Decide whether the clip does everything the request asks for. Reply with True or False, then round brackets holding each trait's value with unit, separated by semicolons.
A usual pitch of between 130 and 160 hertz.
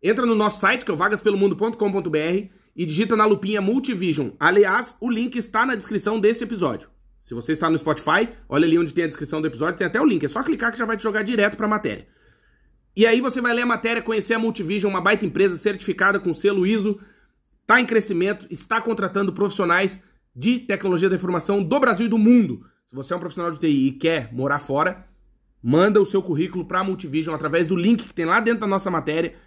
False (200 Hz)